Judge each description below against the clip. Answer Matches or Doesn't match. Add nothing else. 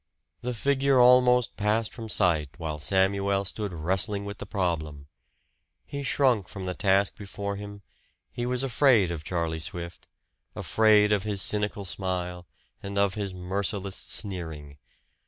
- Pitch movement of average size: Matches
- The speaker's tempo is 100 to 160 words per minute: Matches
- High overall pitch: Doesn't match